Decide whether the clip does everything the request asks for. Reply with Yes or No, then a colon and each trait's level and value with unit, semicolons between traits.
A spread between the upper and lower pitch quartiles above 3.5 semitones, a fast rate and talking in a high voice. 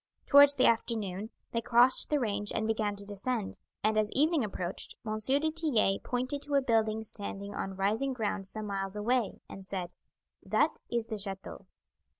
No: average, 4.0 semitones; average, 170 wpm; high, 220 Hz